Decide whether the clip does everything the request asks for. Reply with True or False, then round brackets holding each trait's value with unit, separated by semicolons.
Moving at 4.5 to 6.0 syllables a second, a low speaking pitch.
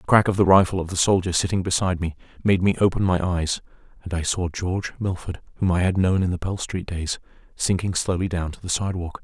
False (6.2 syllables/s; 90 Hz)